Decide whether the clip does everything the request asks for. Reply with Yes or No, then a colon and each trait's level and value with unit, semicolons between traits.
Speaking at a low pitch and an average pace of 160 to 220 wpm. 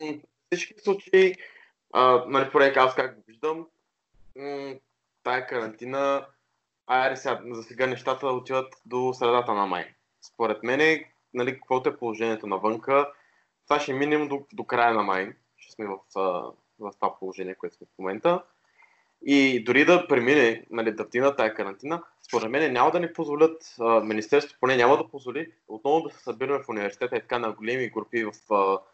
Yes: low, 130 Hz; fast, 165 wpm